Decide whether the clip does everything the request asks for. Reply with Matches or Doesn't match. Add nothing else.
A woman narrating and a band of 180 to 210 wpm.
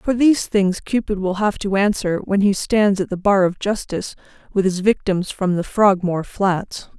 Matches